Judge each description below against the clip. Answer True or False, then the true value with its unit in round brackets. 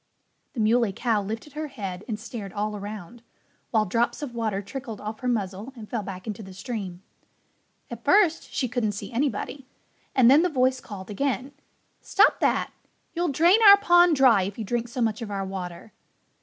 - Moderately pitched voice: False (225 Hz)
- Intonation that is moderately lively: True (4.4 semitones)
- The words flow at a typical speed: True (185 wpm)